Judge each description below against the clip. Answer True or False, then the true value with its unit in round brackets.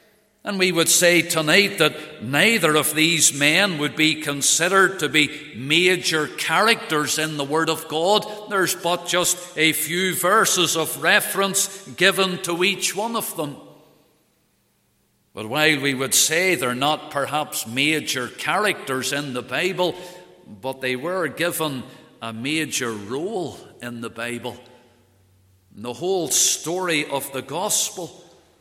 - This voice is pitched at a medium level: True (155 Hz)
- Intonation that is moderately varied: True (4.6 semitones)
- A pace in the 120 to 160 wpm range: True (140 wpm)